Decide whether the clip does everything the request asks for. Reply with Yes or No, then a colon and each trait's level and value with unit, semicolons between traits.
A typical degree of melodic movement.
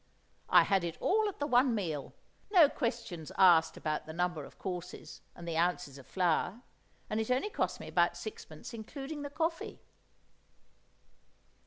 No: wide, 8.7 semitones